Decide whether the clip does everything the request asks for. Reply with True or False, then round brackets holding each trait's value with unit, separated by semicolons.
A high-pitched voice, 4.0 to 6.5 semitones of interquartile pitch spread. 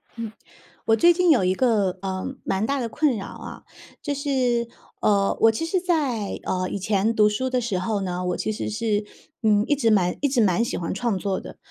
True (220 Hz; 4.7 semitones)